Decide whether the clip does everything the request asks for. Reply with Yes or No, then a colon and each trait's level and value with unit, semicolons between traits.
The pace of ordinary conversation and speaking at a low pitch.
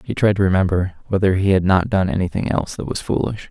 No: fast, 240 wpm; very low, 95 Hz